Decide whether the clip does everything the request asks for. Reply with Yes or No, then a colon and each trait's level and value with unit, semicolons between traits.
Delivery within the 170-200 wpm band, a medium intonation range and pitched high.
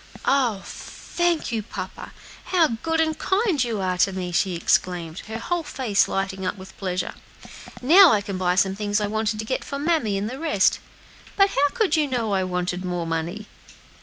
No: average, 190 wpm; wide, 7.5 semitones; high, 215 Hz